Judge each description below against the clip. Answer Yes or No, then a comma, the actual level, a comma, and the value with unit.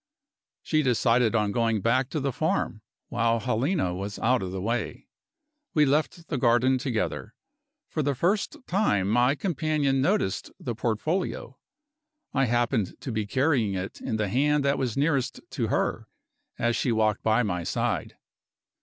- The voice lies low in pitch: Yes, low, 125 Hz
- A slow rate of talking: No, average, 155 wpm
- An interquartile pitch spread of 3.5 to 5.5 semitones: Yes, average, 4.5 semitones